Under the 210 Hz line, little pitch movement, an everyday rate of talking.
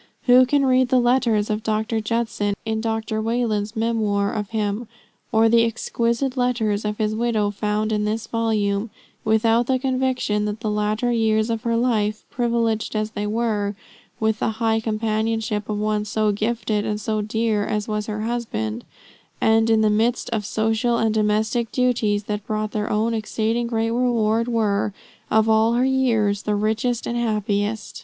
No: high, 220 Hz; narrow, 1.7 semitones; average, 170 wpm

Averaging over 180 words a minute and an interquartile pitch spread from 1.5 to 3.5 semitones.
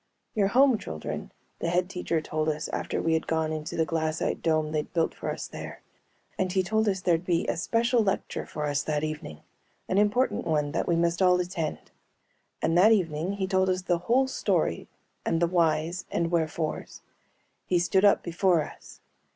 Yes: average, 190 wpm; average, 3.2 semitones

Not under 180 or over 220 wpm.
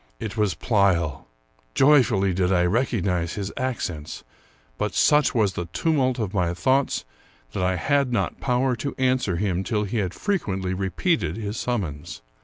No: average, 155 wpm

